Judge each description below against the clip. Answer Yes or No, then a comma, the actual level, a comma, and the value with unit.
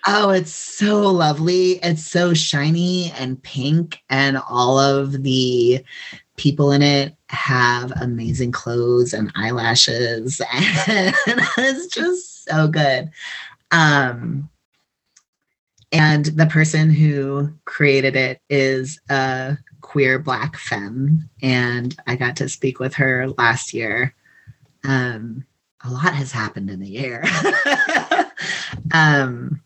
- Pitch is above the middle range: No, medium, 140 Hz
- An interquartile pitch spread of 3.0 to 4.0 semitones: Yes, average, 3.6 semitones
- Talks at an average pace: No, slow, 115 wpm